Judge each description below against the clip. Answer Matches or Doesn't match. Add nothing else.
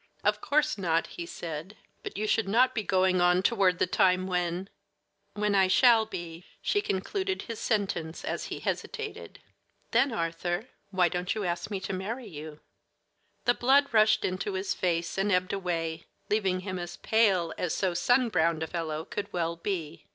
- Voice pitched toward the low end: Doesn't match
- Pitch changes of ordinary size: Matches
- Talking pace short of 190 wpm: Matches